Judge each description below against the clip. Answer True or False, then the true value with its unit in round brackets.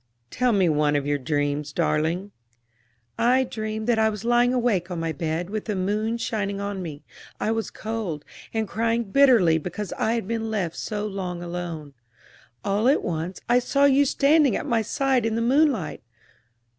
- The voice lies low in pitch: False (210 Hz)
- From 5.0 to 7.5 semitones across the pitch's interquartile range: True (5.3 semitones)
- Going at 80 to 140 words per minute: False (180 wpm)